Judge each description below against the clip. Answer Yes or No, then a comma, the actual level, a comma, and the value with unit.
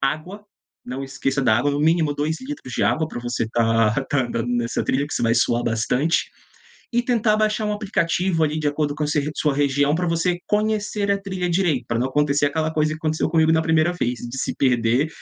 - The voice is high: No, medium, 150 Hz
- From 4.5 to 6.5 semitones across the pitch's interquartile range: Yes, average, 5.2 semitones